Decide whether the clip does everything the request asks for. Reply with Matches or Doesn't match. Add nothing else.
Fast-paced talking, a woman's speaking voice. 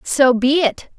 Doesn't match